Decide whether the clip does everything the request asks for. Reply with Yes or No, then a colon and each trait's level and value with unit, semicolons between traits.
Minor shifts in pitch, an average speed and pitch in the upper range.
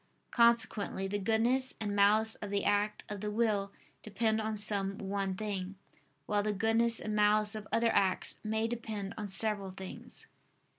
Yes: narrow, 1.7 semitones; average, 160 wpm; high, 210 Hz